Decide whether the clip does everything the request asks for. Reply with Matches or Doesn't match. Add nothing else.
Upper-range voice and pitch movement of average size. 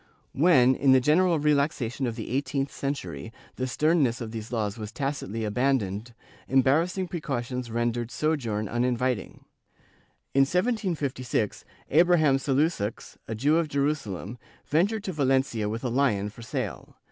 Doesn't match